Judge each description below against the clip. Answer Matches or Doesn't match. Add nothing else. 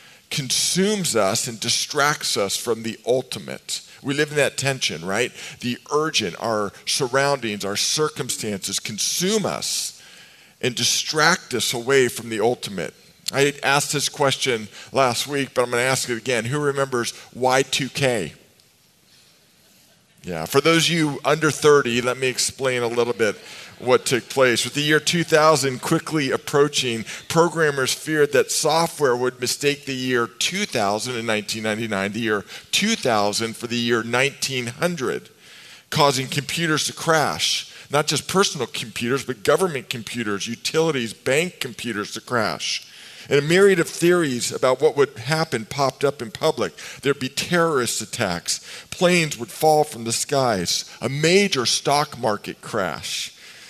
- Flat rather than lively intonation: Doesn't match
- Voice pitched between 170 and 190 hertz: Doesn't match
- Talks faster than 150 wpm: Doesn't match